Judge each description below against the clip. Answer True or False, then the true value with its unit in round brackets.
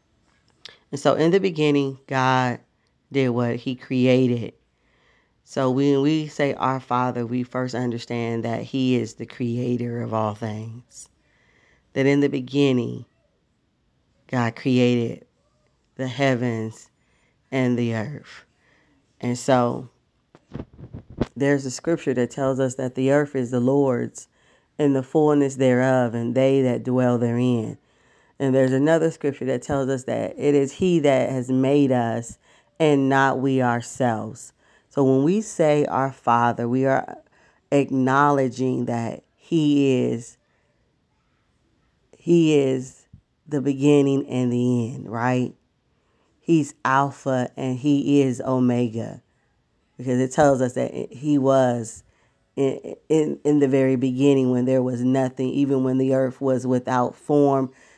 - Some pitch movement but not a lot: False (2.3 semitones)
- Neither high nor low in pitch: False (130 Hz)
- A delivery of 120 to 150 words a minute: True (135 wpm)